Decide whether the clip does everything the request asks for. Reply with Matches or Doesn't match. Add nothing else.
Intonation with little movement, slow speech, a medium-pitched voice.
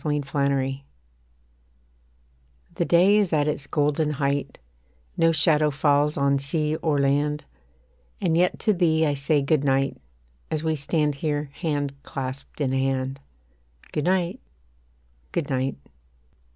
Matches